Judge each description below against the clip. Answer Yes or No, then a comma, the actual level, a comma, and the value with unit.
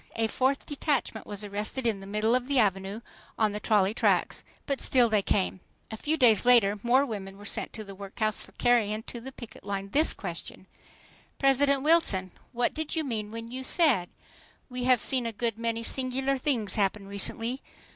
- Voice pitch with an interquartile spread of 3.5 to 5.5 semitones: Yes, average, 4.1 semitones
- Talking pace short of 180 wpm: No, average, 190 wpm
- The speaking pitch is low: No, high, 230 Hz